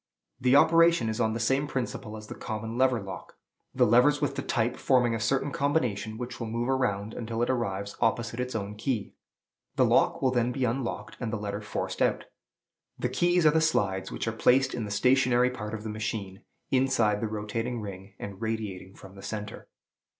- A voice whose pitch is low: Yes, low, 115 Hz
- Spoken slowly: No, average, 200 wpm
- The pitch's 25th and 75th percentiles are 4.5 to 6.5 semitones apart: No, average, 3.4 semitones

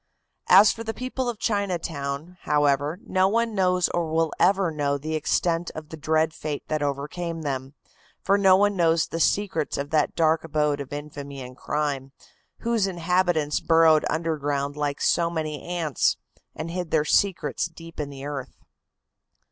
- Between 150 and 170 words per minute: Yes, average, 165 wpm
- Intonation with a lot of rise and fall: No, average, 3.5 semitones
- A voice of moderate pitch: Yes, medium, 160 Hz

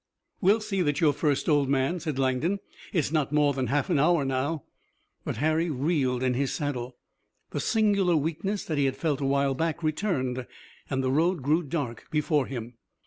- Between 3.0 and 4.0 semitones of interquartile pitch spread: Yes, average, 3.7 semitones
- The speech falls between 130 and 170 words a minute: No, average, 190 wpm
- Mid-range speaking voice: Yes, medium, 145 Hz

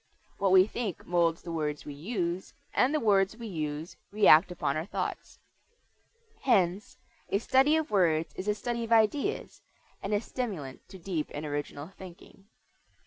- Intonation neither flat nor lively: Yes, average, 5.0 semitones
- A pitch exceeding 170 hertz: Yes, high, 190 Hz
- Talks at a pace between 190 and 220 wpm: No, average, 160 wpm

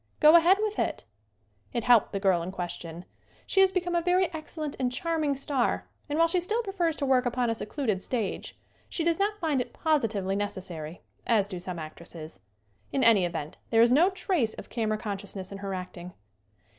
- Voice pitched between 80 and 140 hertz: No, high, 240 Hz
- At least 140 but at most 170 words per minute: No, average, 195 wpm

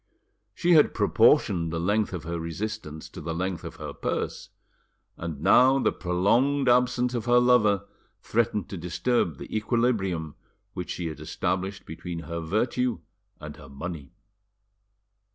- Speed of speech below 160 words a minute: Yes, average, 145 wpm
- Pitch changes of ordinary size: No, wide, 6.5 semitones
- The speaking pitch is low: Yes, very low, 95 Hz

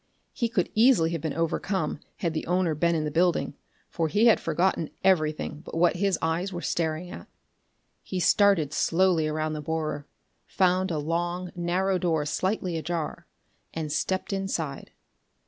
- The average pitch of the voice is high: No, medium, 170 Hz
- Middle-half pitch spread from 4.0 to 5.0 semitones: No, average, 3.0 semitones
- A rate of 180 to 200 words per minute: No, average, 160 wpm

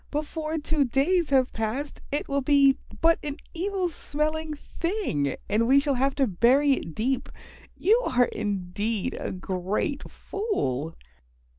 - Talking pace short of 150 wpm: Yes, average, 140 wpm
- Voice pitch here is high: Yes, very high, 275 Hz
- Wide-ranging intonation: Yes, wide, 5.8 semitones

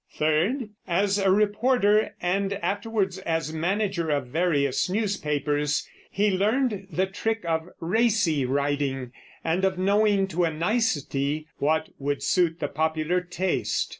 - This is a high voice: No, medium, 180 Hz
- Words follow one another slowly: Yes, slow, 130 wpm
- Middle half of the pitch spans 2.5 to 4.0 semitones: No, average, 4.6 semitones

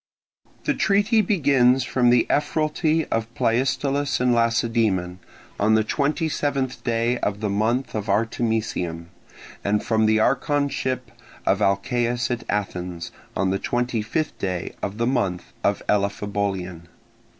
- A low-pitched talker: Yes, low, 115 Hz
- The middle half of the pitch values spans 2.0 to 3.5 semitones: No, average, 4.5 semitones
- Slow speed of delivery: Yes, slow, 125 wpm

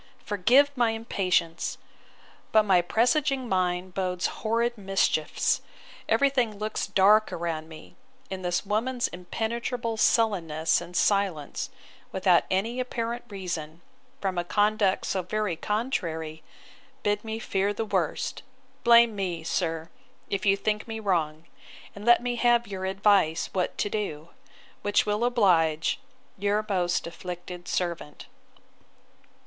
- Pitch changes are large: No, average, 4.2 semitones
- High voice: Yes, high, 200 Hz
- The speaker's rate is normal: No, slow, 125 wpm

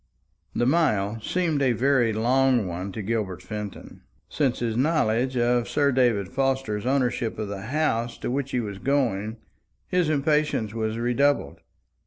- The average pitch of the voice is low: Yes, low, 120 Hz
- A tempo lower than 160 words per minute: Yes, average, 150 wpm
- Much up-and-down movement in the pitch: No, average, 4.1 semitones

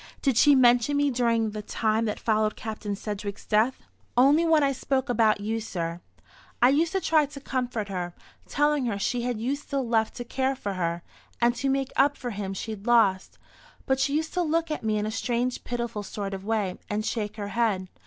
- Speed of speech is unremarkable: No, fast, 210 wpm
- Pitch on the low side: No, high, 235 Hz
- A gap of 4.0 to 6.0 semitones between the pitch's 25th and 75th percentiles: Yes, average, 4.4 semitones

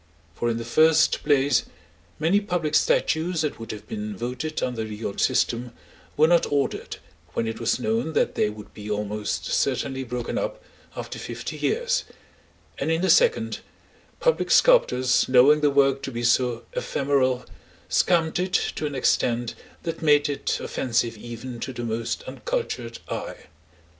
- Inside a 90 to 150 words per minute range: No, average, 160 wpm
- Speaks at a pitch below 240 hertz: Yes, low, 135 Hz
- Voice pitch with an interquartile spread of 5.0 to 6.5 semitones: Yes, wide, 5.5 semitones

